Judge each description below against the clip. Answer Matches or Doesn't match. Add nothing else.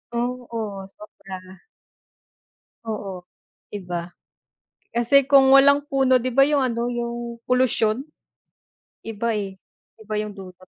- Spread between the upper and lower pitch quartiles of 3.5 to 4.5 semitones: Matches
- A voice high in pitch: Matches